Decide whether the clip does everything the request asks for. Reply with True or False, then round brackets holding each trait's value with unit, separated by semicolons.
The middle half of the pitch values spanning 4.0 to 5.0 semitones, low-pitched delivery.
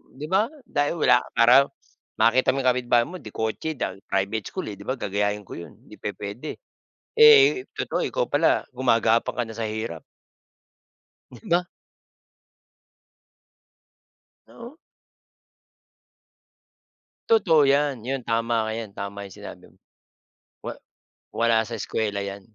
True (4.7 semitones; 115 Hz)